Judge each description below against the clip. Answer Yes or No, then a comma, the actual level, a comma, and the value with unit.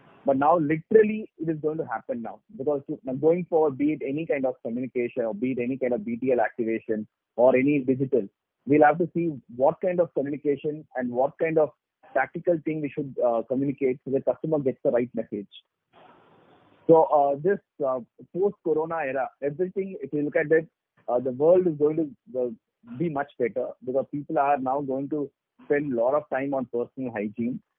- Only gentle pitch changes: No, average, 3.8 semitones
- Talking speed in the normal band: Yes, average, 190 wpm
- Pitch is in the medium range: Yes, medium, 145 Hz